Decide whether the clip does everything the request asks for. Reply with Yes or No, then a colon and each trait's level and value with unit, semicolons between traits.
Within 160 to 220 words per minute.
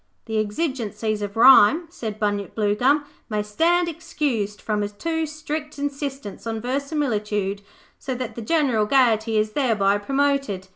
No: average, 140 wpm